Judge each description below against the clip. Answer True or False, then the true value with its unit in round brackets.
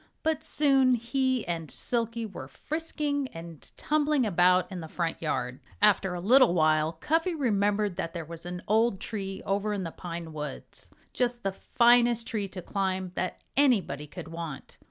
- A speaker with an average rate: True (165 wpm)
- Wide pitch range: True (6.4 semitones)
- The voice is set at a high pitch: True (195 Hz)